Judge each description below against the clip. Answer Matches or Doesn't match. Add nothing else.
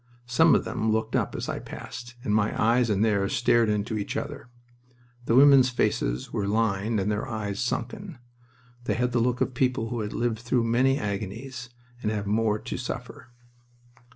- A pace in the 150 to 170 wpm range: Doesn't match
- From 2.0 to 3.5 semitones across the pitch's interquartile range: Matches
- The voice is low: Matches